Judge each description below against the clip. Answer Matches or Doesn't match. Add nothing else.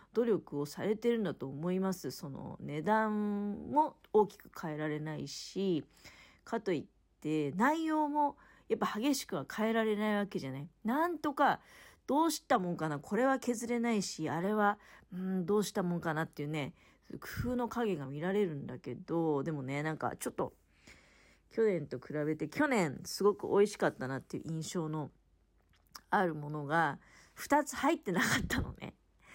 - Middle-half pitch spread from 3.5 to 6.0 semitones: Doesn't match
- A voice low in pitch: Doesn't match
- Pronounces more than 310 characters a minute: Matches